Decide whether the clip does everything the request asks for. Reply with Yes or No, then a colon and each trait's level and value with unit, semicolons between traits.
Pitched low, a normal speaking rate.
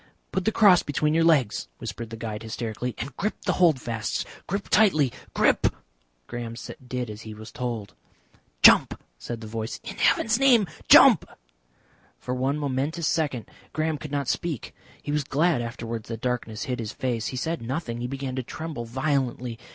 Yes: low, 130 Hz; average, 170 wpm